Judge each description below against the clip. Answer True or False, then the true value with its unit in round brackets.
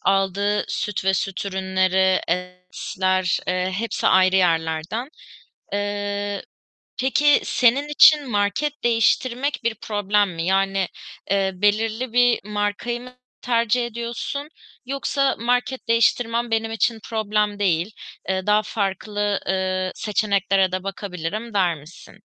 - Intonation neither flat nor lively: True (3.7 semitones)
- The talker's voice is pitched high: True (205 Hz)